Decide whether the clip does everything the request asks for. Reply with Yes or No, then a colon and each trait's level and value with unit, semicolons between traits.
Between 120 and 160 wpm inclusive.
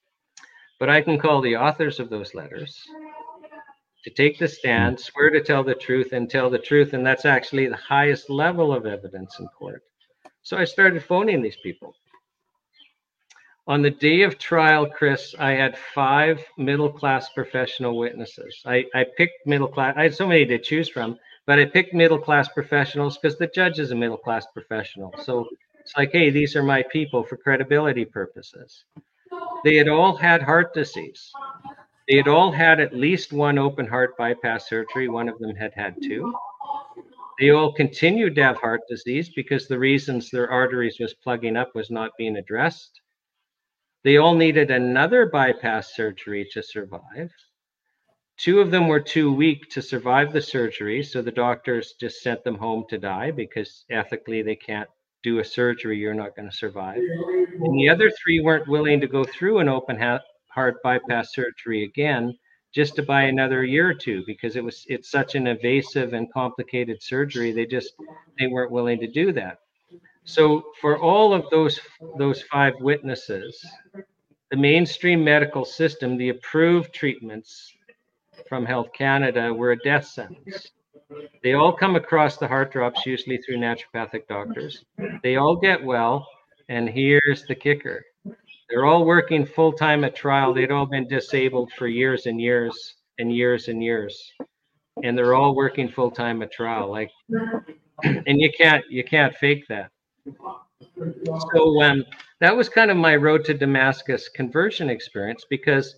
No: average, 170 wpm